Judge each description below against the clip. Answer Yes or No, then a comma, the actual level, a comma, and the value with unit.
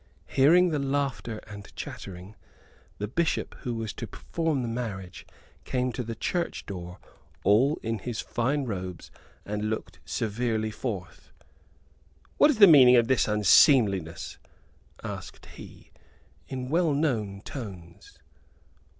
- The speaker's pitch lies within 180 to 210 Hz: No, low, 115 Hz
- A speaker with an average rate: No, slow, 125 wpm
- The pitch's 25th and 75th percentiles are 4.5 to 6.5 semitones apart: Yes, average, 5.1 semitones